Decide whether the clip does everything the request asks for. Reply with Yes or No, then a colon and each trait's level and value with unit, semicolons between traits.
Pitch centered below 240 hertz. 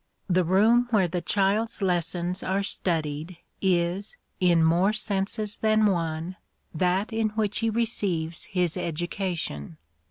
Yes: medium, 185 Hz